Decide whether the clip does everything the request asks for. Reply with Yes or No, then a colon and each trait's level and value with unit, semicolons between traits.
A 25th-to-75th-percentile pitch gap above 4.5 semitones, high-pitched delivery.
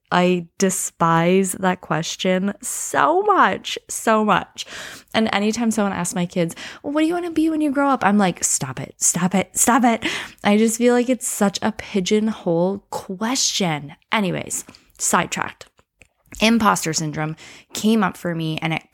Yes: average, 5.0 semitones; high, 200 Hz